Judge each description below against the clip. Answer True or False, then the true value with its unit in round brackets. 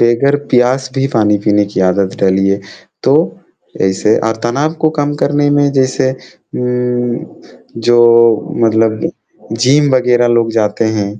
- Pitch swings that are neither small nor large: True (3.6 semitones)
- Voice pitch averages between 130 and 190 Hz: False (120 Hz)